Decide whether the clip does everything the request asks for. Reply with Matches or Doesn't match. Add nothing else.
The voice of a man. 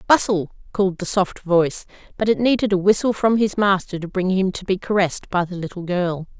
Doesn't match